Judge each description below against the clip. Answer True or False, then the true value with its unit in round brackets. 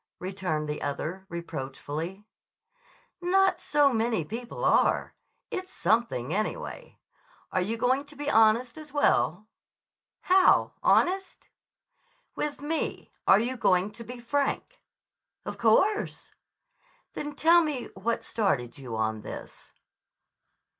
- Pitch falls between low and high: False (230 Hz)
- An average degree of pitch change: False (8.4 semitones)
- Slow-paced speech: True (120 wpm)